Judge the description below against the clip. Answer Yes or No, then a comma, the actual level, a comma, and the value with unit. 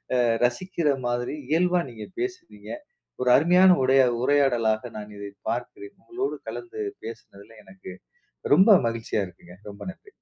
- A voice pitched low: Yes, low, 130 Hz